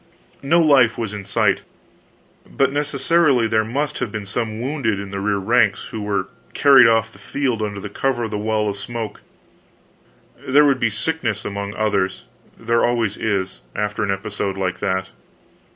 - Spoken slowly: No, average, 170 wpm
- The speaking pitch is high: No, low, 110 Hz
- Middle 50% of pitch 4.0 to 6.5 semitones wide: No, average, 3.5 semitones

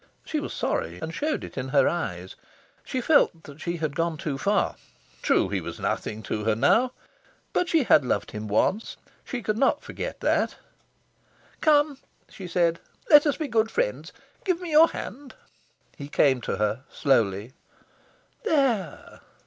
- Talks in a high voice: No, medium, 175 Hz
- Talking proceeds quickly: No, average, 160 wpm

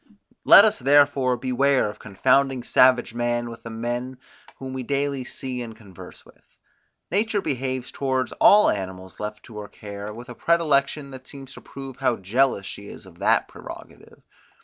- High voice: No, low, 125 Hz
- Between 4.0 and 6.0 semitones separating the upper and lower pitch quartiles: No, average, 3.4 semitones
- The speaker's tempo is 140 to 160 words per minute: No, average, 170 wpm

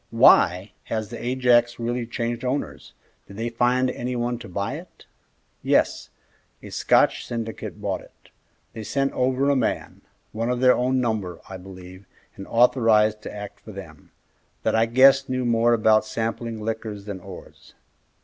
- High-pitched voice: No, low, 115 Hz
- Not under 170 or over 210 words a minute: No, average, 160 wpm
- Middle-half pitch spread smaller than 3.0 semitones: Yes, narrow, 2.5 semitones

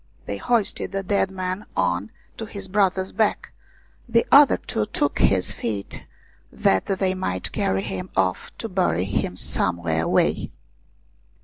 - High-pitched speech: No, medium, 180 Hz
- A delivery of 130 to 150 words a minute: Yes, average, 145 wpm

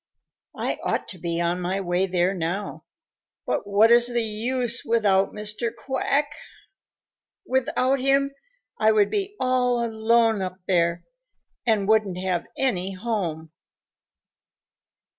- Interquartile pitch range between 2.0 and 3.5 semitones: No, average, 4.6 semitones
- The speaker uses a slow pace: Yes, slow, 120 wpm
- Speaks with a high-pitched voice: Yes, high, 215 Hz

